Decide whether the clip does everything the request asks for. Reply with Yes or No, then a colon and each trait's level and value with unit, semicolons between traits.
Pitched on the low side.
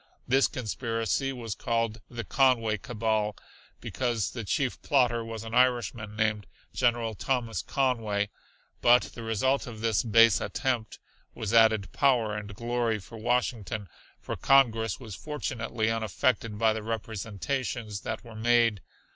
Yes: low, 115 Hz